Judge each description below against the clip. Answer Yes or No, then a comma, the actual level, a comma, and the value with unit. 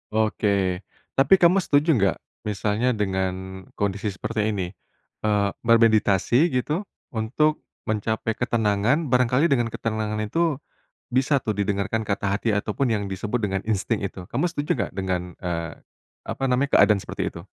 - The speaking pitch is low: Yes, low, 110 Hz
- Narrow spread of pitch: No, average, 3.9 semitones